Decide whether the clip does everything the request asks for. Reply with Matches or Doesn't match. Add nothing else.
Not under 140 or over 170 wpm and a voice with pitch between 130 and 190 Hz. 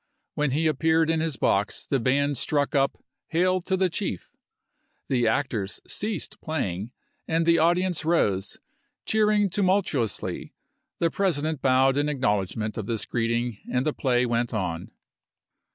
Matches